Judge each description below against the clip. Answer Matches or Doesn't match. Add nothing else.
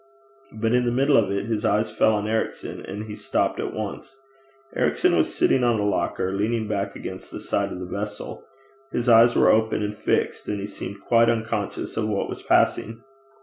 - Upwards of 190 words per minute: Matches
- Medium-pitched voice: Doesn't match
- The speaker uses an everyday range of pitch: Doesn't match